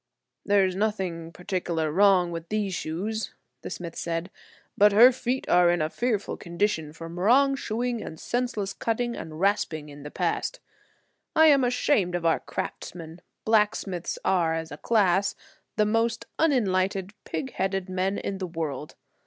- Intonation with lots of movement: No, average, 4.5 semitones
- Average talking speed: Yes, average, 155 wpm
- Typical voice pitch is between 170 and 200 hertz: Yes, high, 190 Hz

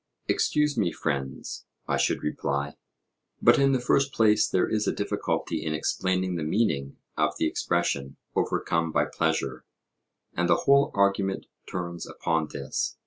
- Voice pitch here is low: Yes, very low, 85 Hz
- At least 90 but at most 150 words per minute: Yes, average, 145 wpm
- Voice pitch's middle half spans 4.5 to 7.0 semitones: Yes, wide, 5.6 semitones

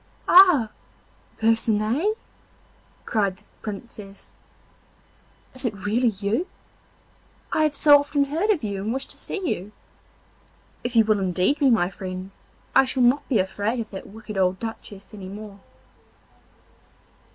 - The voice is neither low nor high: No, high, 220 Hz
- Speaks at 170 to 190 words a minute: No, average, 140 wpm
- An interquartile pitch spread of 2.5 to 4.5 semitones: No, average, 5.1 semitones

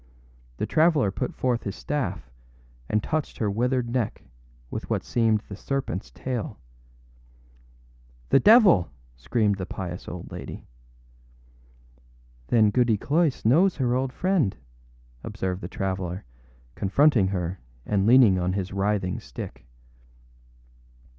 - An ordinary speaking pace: No, slow, 120 wpm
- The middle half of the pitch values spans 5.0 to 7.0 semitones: Yes, wide, 5.5 semitones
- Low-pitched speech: Yes, low, 110 Hz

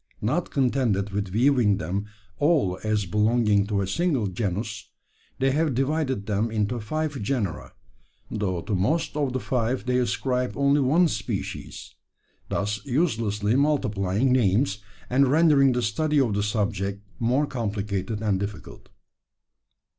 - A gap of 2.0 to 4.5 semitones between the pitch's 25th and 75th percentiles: No, average, 4.9 semitones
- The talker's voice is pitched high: No, low, 115 Hz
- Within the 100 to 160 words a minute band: Yes, slow, 135 wpm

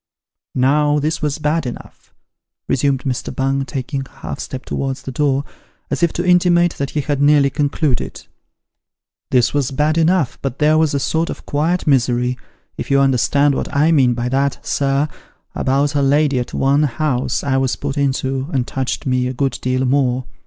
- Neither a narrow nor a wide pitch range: No, narrow, 2.1 semitones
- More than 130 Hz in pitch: Yes, medium, 140 Hz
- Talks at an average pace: Yes, average, 190 wpm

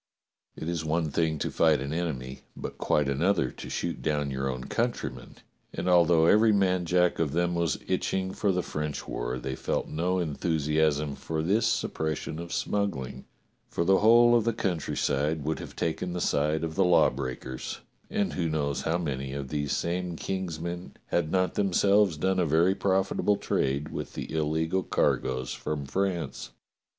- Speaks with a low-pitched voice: Yes, very low, 80 Hz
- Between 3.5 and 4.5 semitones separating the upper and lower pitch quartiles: Yes, average, 3.9 semitones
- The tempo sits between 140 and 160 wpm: No, average, 180 wpm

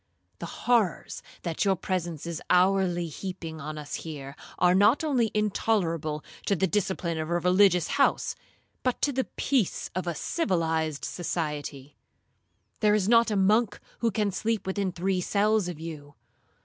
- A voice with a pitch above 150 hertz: Yes, medium, 185 Hz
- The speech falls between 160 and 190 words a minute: No, average, 150 wpm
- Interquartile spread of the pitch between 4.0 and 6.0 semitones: Yes, average, 4.3 semitones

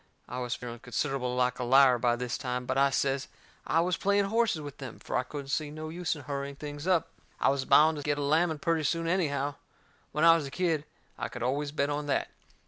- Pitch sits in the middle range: Yes, medium, 145 Hz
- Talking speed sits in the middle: No, fast, 235 wpm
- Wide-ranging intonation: No, average, 3.4 semitones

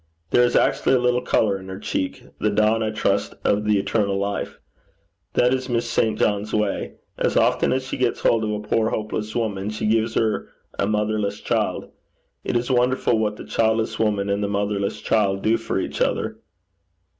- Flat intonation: Yes, narrow, 1.9 semitones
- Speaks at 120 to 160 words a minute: No, average, 190 wpm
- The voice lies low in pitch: Yes, low, 110 Hz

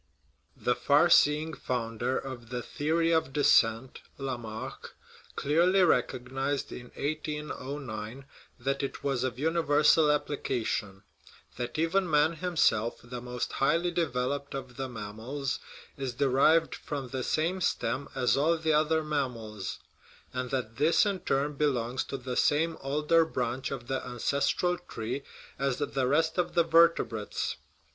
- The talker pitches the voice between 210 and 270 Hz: No, low, 135 Hz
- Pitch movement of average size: Yes, average, 3.8 semitones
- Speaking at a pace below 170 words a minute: Yes, average, 140 wpm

